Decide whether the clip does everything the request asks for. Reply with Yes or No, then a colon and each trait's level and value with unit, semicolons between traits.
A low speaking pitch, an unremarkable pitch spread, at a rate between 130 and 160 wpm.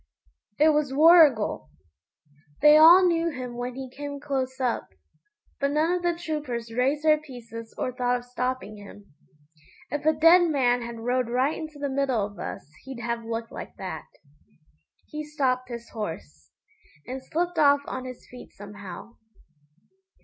No: very high, 255 Hz; average, 4.2 semitones; average, 155 wpm